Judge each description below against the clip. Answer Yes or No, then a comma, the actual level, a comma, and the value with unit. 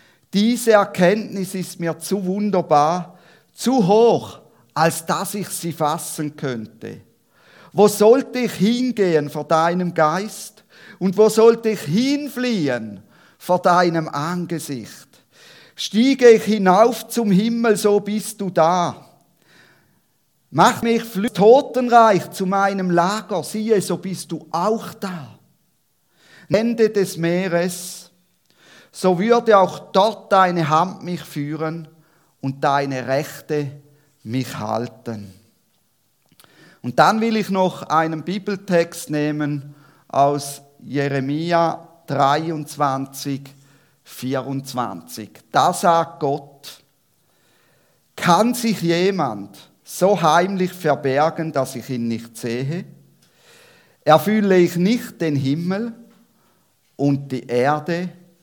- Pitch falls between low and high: Yes, medium, 175 Hz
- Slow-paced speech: Yes, slow, 105 wpm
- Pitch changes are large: Yes, wide, 5.9 semitones